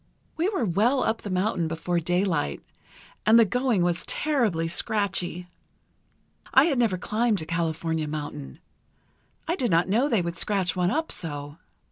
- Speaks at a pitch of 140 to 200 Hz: Yes, medium, 185 Hz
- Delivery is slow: No, average, 155 wpm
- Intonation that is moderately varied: No, wide, 5.7 semitones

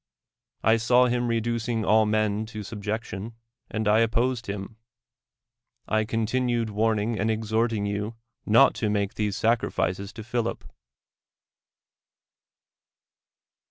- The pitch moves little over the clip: Yes, narrow, 1.7 semitones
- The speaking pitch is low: Yes, low, 110 Hz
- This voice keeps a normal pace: No, slow, 115 wpm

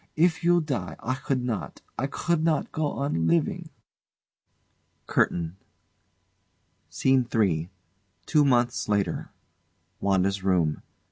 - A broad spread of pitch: Yes, wide, 8.3 semitones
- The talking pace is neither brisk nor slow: No, slow, 110 wpm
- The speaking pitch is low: Yes, low, 125 Hz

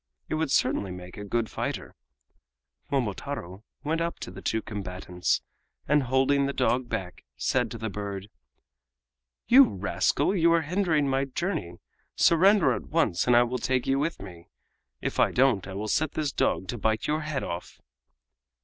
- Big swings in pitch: Yes, wide, 7.3 semitones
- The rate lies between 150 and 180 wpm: Yes, average, 170 wpm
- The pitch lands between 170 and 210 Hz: No, low, 125 Hz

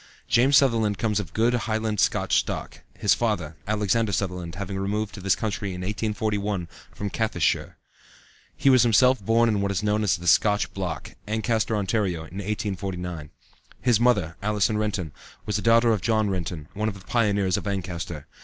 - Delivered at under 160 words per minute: No, average, 175 wpm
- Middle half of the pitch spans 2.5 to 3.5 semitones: Yes, average, 2.8 semitones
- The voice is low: Yes, low, 105 Hz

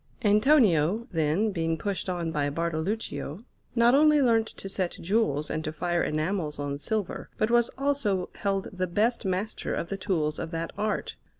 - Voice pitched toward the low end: No, medium, 185 Hz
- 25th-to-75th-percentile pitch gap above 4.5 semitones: Yes, average, 5.2 semitones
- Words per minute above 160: Yes, average, 170 wpm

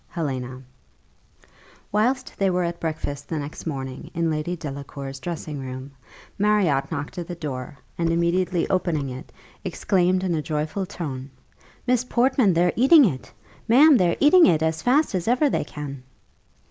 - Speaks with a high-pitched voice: No, medium, 170 Hz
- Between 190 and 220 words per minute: No, average, 155 wpm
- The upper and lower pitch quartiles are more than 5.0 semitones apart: Yes, wide, 5.5 semitones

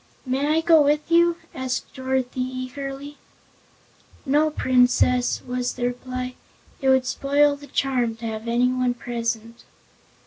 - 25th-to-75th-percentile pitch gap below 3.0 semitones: Yes, narrow, 2.4 semitones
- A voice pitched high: Yes, very high, 255 Hz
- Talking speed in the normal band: No, slow, 130 wpm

